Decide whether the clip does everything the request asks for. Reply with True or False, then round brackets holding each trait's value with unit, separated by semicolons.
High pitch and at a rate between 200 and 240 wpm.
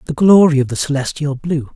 False (150 Hz; 205 wpm)